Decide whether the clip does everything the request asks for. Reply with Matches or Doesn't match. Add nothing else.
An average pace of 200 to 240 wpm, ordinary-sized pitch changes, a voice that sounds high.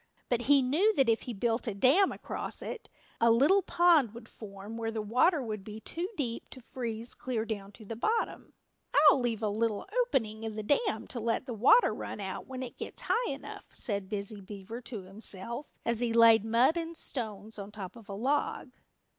Matches